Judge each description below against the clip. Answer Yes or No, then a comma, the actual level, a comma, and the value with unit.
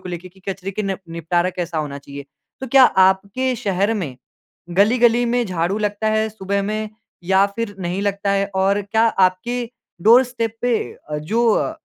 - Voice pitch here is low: No, high, 200 Hz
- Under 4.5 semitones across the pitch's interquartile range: Yes, average, 3.5 semitones